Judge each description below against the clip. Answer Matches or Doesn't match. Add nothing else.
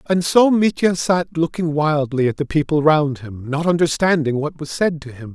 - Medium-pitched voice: Matches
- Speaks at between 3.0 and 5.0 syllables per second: Matches